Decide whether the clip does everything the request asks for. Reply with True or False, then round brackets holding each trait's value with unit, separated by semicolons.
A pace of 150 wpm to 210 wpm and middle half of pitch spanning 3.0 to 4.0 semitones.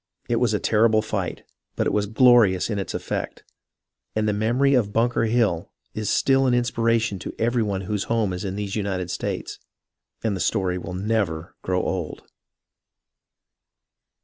True (165 wpm; 3.3 semitones)